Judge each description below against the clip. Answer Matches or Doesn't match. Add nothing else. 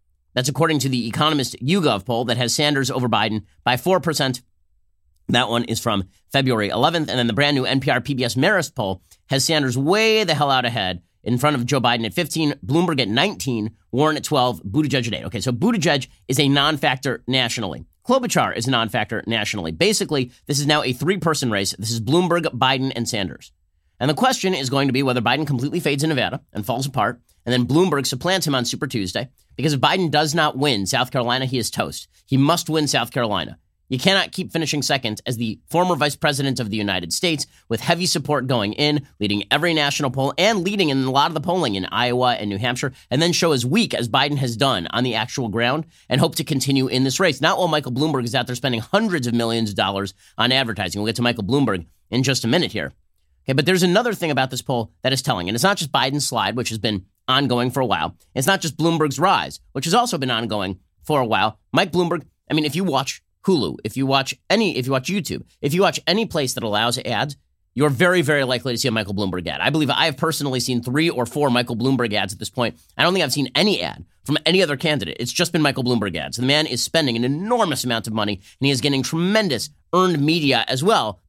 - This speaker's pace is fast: Matches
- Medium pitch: Doesn't match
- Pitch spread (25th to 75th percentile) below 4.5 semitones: Doesn't match